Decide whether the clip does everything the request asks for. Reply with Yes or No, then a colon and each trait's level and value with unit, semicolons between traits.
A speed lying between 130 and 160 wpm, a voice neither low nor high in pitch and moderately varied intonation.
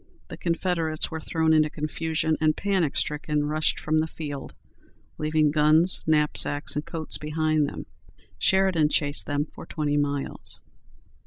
No: average, 140 wpm; medium, 155 Hz; narrow, 1.2 semitones